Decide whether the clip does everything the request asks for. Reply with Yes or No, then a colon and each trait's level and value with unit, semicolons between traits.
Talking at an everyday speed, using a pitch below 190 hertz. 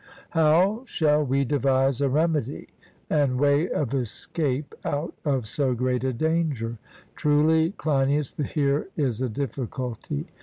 No: slow, 125 wpm; medium, 140 Hz